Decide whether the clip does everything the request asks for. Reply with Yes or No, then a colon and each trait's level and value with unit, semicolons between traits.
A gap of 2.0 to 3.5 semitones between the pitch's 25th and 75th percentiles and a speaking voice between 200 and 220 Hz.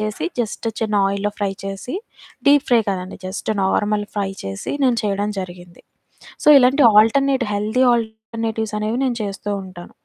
Yes: average, 2.8 semitones; high, 210 Hz